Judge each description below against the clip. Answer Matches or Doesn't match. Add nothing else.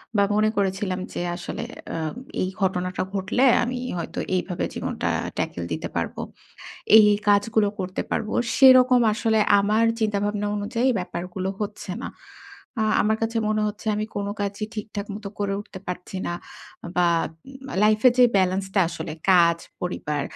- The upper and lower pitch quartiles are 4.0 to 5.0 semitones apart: Doesn't match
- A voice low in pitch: Doesn't match